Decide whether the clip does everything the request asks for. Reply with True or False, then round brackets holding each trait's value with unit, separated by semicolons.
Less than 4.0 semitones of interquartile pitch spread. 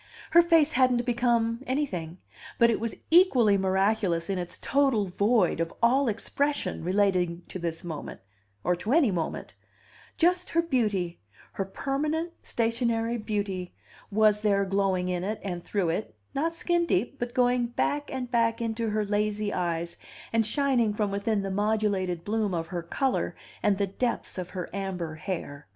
False (4.7 semitones)